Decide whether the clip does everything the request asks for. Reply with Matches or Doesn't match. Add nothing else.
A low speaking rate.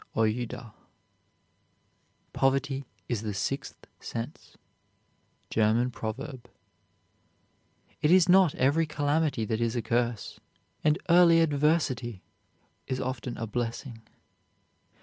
Matches